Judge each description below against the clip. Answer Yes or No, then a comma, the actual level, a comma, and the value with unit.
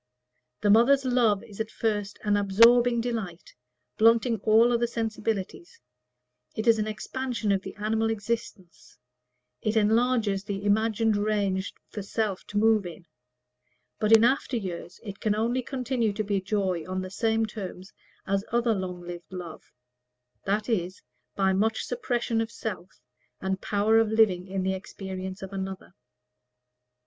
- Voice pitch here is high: Yes, high, 215 Hz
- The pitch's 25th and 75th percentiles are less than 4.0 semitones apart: Yes, average, 2.8 semitones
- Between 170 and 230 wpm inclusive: No, average, 150 wpm